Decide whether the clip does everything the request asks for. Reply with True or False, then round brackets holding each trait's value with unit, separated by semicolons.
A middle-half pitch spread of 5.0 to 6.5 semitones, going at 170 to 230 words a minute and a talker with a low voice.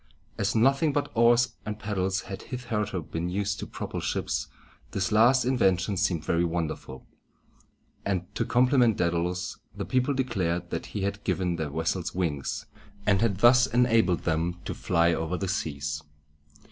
False (5.3 semitones; 155 wpm; 95 Hz)